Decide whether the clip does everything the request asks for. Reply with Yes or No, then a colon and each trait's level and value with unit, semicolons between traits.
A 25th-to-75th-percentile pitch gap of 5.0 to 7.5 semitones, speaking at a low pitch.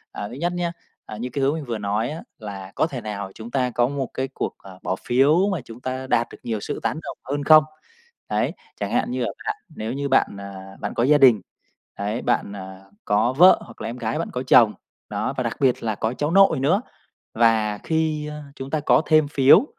Yes: wide, 5.4 semitones; low, 125 Hz